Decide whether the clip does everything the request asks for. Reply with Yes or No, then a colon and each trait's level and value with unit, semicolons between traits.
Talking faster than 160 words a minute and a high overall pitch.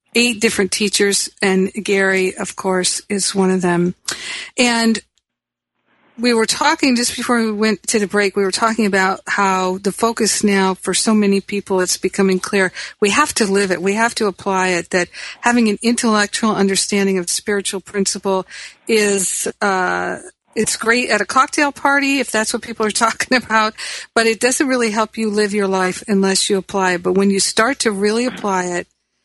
Yes: average, 180 wpm; high, 205 Hz